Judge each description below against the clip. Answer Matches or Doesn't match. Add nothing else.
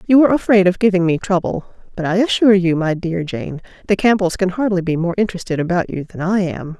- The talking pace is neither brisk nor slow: Doesn't match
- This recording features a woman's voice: Matches